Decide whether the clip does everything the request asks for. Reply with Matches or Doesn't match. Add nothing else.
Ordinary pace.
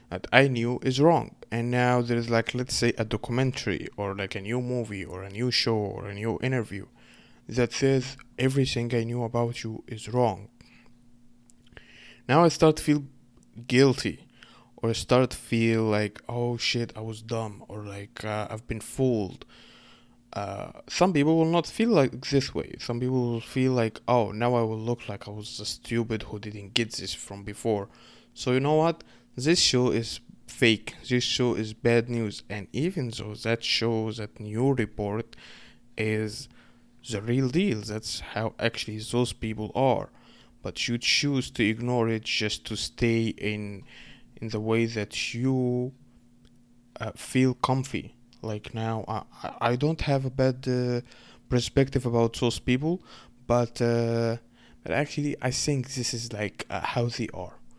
Matches